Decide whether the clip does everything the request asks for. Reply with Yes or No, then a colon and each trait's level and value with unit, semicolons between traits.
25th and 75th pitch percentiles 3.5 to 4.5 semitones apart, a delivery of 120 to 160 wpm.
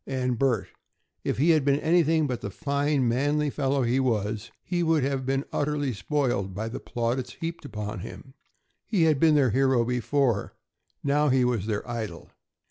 No: average, 3.9 semitones; average, 175 wpm